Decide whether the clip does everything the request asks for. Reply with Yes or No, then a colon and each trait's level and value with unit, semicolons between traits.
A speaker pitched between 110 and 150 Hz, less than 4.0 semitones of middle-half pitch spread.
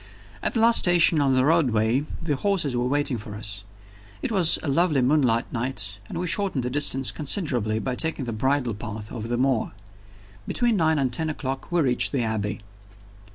No: low, 135 Hz; wide, 5.4 semitones